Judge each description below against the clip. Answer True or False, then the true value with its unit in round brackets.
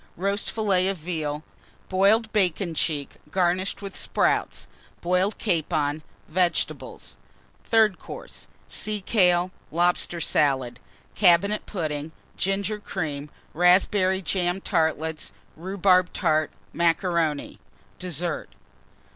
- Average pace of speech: False (95 wpm)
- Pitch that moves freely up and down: False (3.4 semitones)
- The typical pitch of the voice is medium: True (180 Hz)